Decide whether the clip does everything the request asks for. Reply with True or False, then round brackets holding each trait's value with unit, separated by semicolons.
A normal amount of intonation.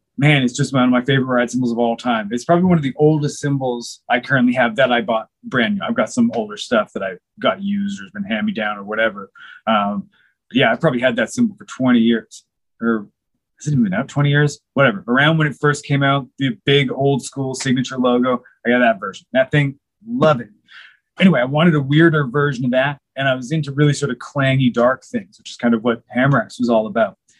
True (3.8 semitones)